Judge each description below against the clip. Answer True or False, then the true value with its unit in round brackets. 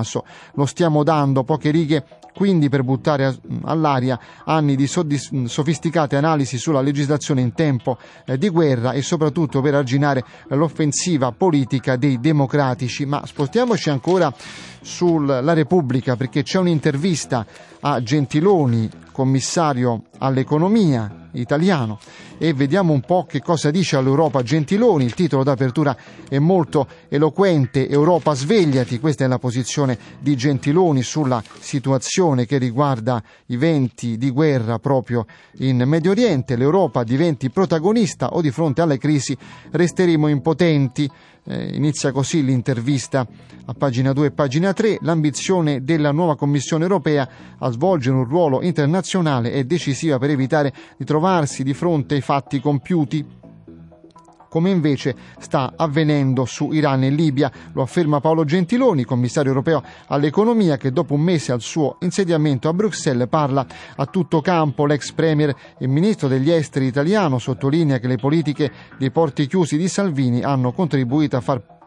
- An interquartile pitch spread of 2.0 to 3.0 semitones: False (3.5 semitones)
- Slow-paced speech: False (135 wpm)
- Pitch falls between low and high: True (145 Hz)